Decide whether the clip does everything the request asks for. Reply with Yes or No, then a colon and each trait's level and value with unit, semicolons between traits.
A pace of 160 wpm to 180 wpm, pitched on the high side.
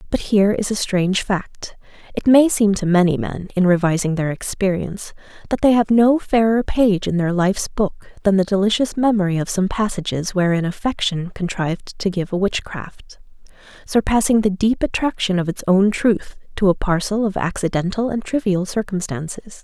Yes: average, 170 wpm; high, 195 Hz